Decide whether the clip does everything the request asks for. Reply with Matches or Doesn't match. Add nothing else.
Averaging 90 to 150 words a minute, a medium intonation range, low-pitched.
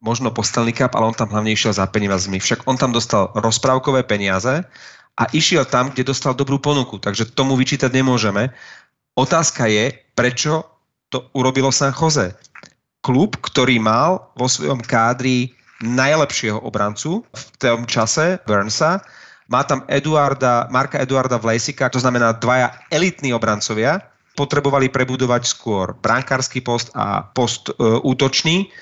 Matches